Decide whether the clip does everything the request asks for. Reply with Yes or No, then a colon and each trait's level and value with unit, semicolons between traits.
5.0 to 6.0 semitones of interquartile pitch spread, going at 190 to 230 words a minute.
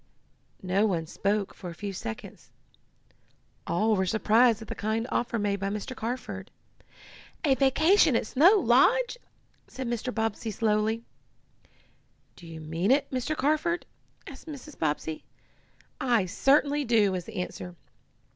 No: average, 5.3 semitones; slow, 135 wpm